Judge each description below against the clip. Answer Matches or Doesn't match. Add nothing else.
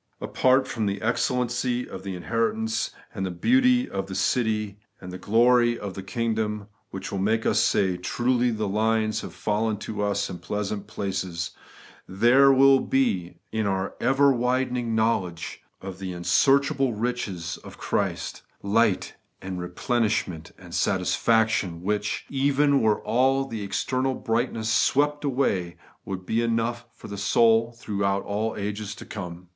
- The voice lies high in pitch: Doesn't match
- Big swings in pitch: Doesn't match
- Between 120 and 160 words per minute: Matches